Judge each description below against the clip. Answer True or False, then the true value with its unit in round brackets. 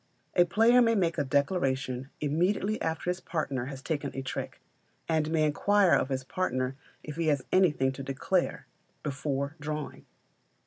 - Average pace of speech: True (160 wpm)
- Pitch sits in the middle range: True (150 Hz)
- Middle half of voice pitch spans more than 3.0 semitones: True (4.7 semitones)